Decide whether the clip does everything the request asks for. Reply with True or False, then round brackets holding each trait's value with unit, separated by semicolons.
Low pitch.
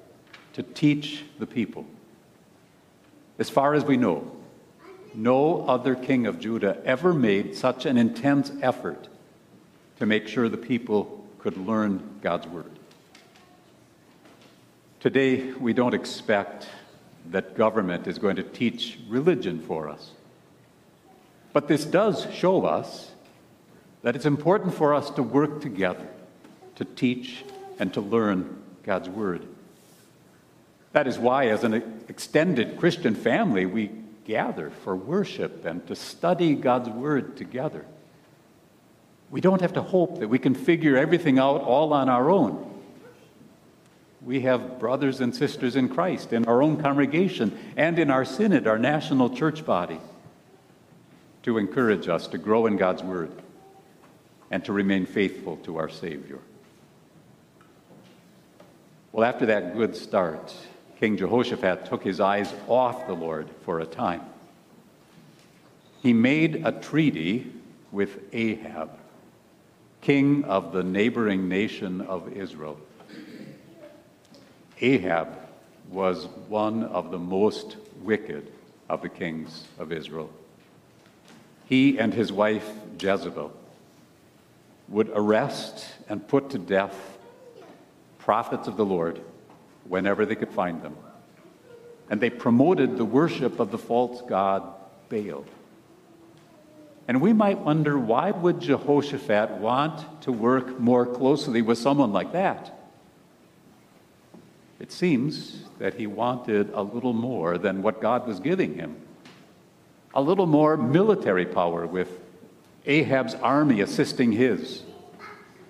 True (120 Hz)